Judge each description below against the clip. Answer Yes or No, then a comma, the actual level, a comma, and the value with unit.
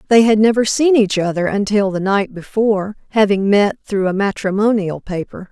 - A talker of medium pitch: No, high, 205 Hz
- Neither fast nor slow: Yes, average, 175 wpm